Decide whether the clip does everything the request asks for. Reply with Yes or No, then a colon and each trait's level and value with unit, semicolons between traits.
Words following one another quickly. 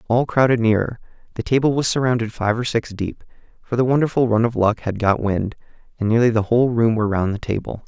Yes: fast, 220 wpm